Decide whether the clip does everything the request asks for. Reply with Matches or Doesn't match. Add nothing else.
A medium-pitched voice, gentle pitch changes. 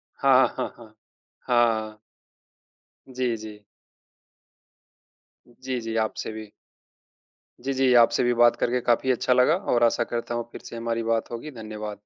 Doesn't match